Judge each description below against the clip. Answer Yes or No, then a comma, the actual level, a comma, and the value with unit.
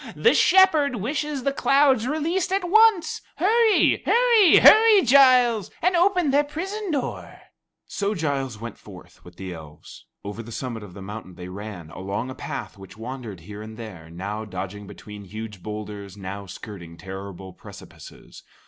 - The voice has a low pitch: Yes, low, 115 Hz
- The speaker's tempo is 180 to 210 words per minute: No, average, 155 wpm